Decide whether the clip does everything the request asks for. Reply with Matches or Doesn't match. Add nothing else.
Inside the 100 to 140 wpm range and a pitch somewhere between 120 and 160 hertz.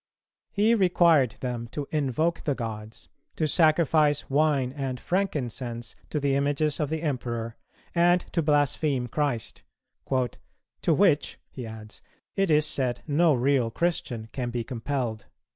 Matches